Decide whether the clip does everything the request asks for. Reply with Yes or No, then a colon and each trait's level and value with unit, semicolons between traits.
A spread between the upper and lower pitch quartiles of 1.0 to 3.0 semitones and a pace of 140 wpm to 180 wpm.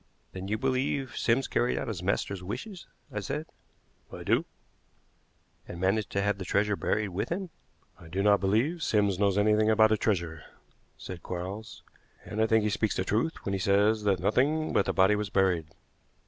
No: narrow, 2.5 semitones; average, 190 wpm